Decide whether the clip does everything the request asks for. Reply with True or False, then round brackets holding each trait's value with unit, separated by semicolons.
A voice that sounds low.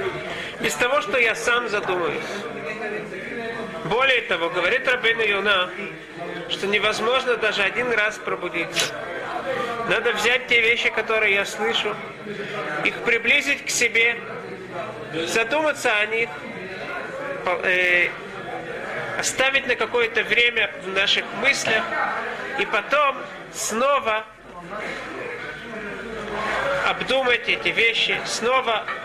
False (225 Hz)